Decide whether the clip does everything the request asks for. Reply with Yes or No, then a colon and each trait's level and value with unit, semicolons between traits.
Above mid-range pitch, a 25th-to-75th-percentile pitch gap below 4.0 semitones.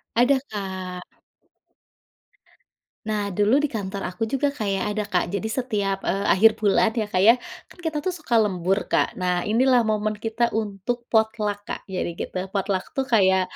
Yes: high, 210 Hz; average, 2.7 semitones